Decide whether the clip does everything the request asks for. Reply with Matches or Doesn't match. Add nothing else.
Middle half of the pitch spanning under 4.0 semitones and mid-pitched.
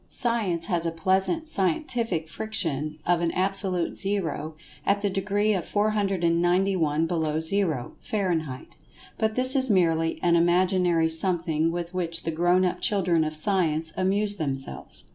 Matches